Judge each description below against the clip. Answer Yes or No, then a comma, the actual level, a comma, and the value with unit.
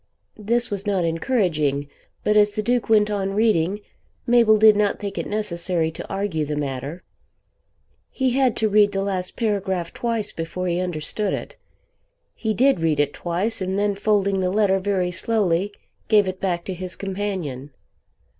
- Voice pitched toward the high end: Yes, high, 195 Hz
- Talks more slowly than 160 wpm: No, average, 165 wpm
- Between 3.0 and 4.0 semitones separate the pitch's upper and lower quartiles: Yes, average, 3.4 semitones